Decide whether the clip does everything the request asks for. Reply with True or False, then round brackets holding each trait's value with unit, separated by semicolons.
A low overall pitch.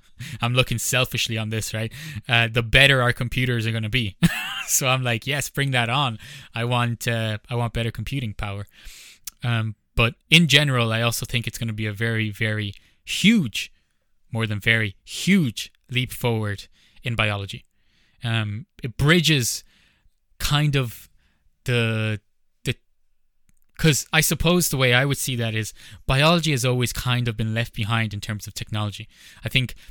True (115 Hz)